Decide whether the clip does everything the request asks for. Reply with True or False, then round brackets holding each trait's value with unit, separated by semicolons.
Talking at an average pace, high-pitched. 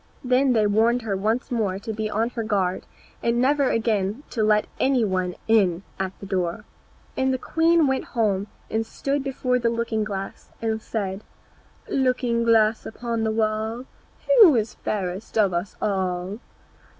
True (160 wpm; 220 Hz)